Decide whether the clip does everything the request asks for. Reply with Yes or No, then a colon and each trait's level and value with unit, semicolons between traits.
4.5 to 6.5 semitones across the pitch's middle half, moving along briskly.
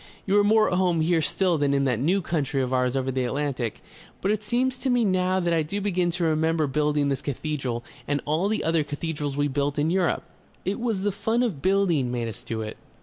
Yes: average, 5.3 semitones; fast, 235 wpm